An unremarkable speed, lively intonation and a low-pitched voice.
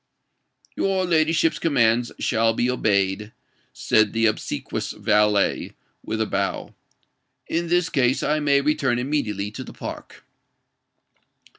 No: slow, 120 wpm; wide, 6.2 semitones; low, 120 Hz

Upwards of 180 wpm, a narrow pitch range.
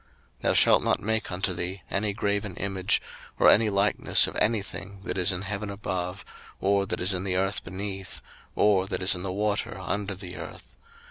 Yes: average, 200 wpm; narrow, 1.6 semitones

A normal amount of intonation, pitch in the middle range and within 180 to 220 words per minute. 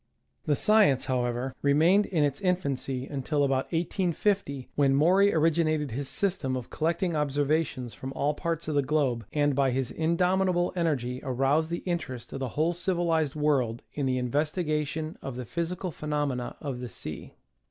No: average, 4.1 semitones; medium, 150 Hz; average, 165 wpm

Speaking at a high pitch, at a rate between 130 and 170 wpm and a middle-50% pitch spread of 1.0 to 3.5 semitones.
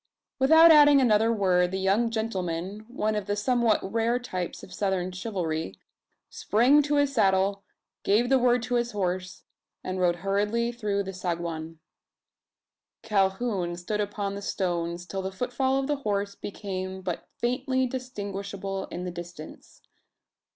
No: high, 200 Hz; average, 145 wpm; average, 4.4 semitones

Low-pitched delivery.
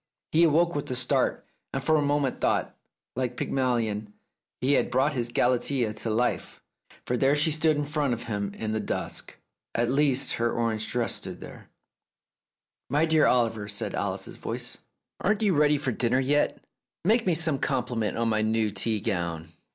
Yes: low, 125 Hz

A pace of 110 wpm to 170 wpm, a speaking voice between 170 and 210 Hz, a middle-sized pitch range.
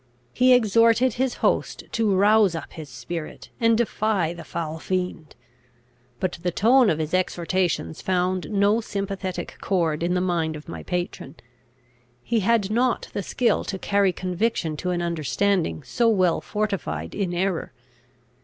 Yes: average, 150 wpm; medium, 185 Hz; average, 4.1 semitones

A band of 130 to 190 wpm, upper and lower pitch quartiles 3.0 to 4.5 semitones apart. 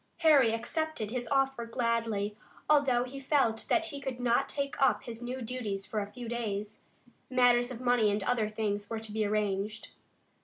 Yes: average, 180 wpm; average, 3.3 semitones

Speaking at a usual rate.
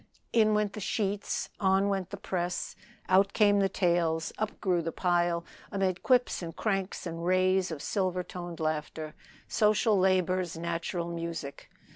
Yes: average, 150 wpm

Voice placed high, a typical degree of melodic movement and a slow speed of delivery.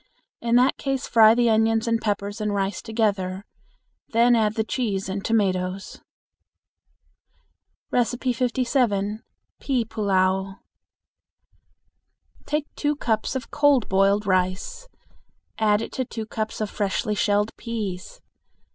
Yes: high, 220 Hz; average, 3.1 semitones; slow, 115 wpm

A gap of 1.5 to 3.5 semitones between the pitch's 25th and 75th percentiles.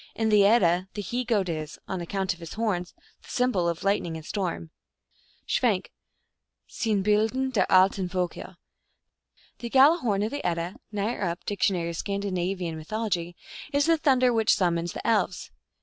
No: average, 4.3 semitones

